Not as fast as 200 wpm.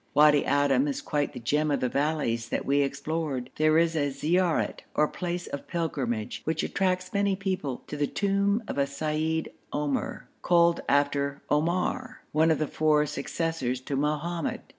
Yes: average, 165 wpm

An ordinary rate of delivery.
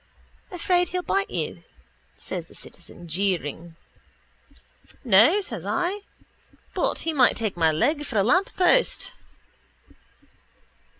No: slow, 110 wpm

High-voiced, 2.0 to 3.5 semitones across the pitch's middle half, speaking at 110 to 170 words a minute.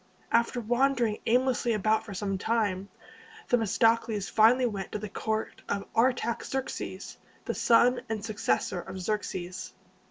Yes: high, 220 Hz; average, 2.8 semitones; slow, 135 wpm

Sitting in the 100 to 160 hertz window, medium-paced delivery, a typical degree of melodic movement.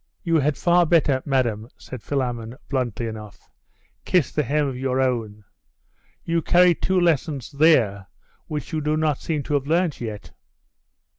Yes: medium, 140 Hz; average, 155 wpm; average, 4.9 semitones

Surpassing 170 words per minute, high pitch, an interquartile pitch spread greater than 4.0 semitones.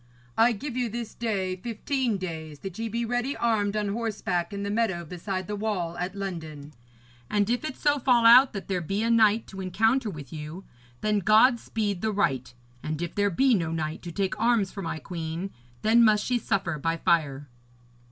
Yes: average, 200 wpm; high, 200 Hz; average, 4.9 semitones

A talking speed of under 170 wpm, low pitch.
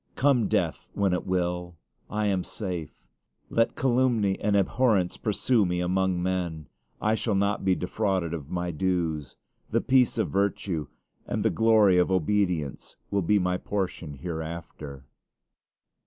Yes: average, 140 wpm; very low, 95 Hz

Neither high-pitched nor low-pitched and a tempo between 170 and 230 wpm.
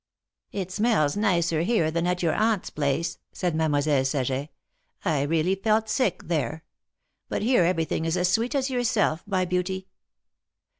No: medium, 180 Hz; average, 160 wpm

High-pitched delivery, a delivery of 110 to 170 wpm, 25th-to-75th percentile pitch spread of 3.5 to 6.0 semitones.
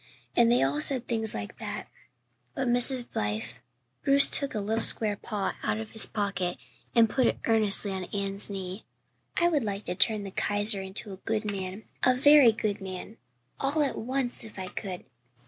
No: high, 210 Hz; average, 185 wpm; average, 3.8 semitones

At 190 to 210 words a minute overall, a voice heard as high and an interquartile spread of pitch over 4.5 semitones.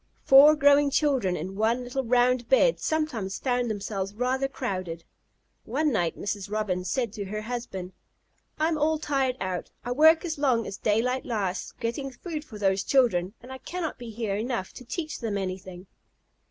No: average, 175 wpm; high, 240 Hz; wide, 5.5 semitones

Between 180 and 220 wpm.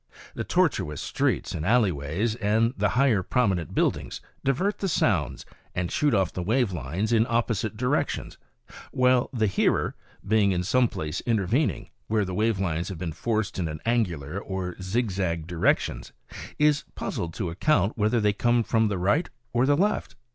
No: average, 170 wpm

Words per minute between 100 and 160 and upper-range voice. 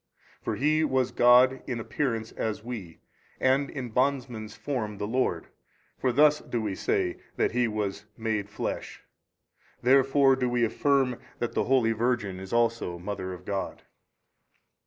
No: average, 155 wpm; low, 120 Hz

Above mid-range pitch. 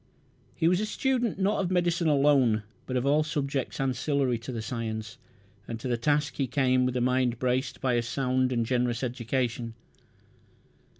No: low, 130 Hz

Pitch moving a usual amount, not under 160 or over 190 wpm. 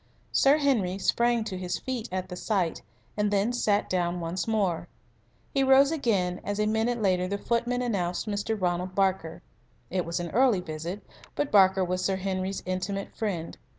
Yes: average, 3.6 semitones; average, 175 wpm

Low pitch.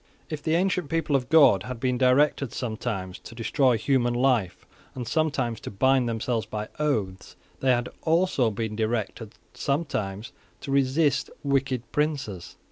Yes: low, 125 Hz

